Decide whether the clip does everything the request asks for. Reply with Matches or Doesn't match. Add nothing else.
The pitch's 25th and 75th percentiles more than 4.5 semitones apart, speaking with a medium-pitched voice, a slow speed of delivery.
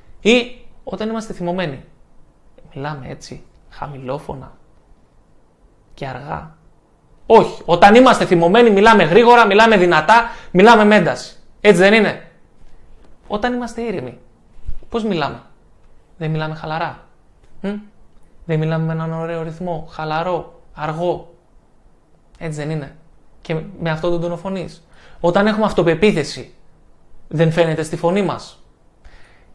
Matches